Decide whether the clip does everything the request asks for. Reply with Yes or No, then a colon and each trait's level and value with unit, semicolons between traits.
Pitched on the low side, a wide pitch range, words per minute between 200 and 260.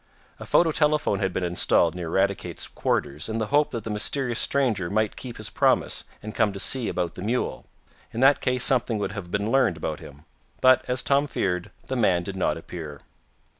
Yes: low, 105 Hz; wide, 6.1 semitones; fast, 205 wpm